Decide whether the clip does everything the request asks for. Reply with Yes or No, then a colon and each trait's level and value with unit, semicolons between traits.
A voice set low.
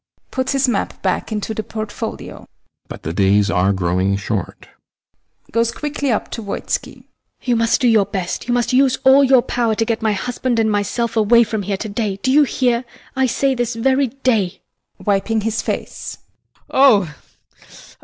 No: high, 225 Hz